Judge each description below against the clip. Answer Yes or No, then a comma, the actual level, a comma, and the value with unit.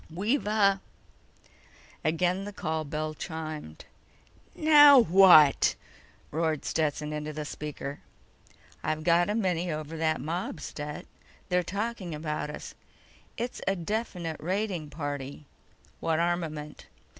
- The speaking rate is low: Yes, slow, 115 wpm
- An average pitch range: Yes, average, 3.9 semitones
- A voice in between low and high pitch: Yes, medium, 165 Hz